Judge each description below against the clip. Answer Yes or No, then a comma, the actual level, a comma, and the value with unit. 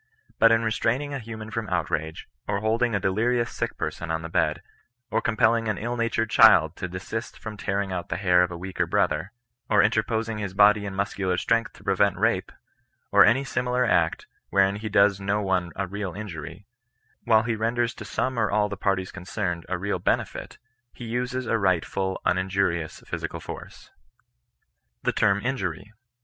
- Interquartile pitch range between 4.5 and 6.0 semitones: No, average, 3.4 semitones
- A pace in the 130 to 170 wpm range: No, average, 180 wpm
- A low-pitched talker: Yes, low, 100 Hz